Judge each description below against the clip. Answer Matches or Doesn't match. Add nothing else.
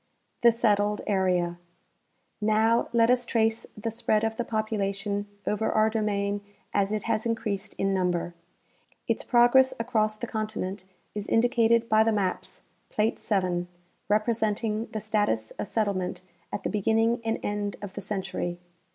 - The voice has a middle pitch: Doesn't match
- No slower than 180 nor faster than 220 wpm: Doesn't match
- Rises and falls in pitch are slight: Matches